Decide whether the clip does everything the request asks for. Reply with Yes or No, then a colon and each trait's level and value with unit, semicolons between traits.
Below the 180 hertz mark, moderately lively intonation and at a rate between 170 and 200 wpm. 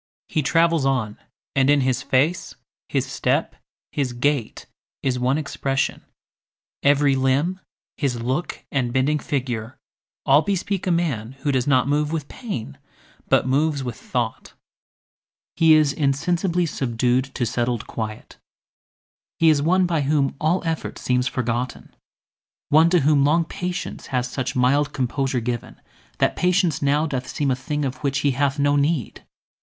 No: medium, 140 Hz; average, 3.5 semitones; average, 150 wpm